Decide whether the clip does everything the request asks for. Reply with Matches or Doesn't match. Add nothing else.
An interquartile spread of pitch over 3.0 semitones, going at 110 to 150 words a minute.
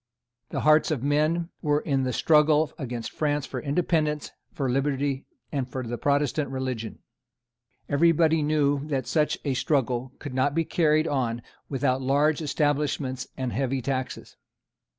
Doesn't match